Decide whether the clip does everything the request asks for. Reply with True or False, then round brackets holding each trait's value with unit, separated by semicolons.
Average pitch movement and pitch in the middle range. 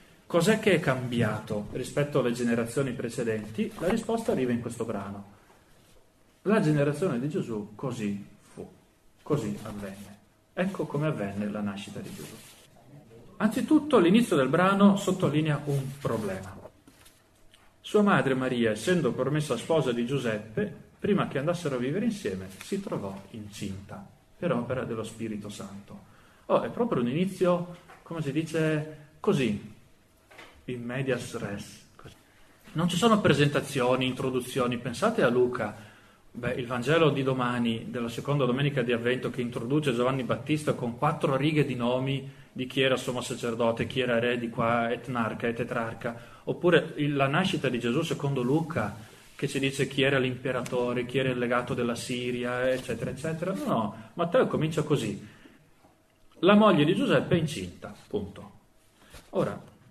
False (4.7 semitones; 125 Hz)